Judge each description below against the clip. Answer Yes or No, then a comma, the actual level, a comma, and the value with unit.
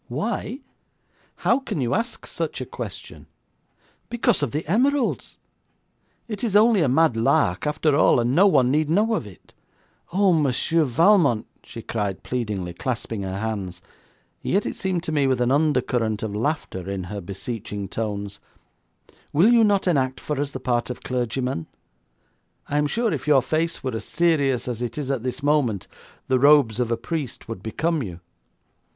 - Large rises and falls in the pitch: Yes, wide, 6.3 semitones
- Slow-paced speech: No, average, 175 wpm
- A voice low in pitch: Yes, low, 130 Hz